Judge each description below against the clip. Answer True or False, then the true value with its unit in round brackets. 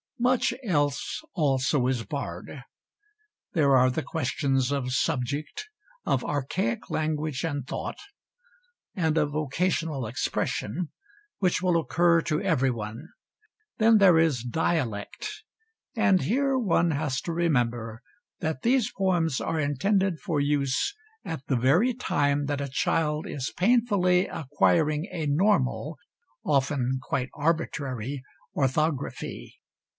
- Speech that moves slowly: True (115 wpm)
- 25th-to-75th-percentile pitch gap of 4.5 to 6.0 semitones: True (4.8 semitones)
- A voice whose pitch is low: False (150 Hz)